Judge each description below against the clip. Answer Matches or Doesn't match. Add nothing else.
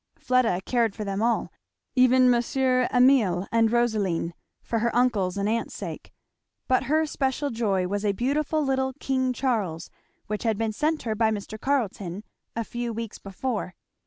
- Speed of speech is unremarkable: Matches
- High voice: Matches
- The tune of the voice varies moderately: Matches